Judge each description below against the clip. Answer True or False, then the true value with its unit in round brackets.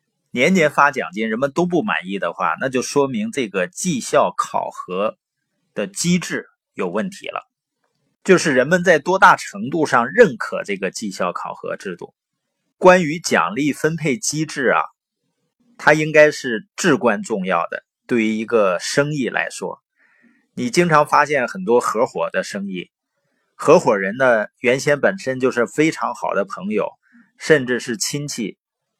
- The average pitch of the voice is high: False (150 Hz)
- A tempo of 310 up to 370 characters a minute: False (225 characters per minute)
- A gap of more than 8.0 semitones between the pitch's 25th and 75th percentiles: False (6.7 semitones)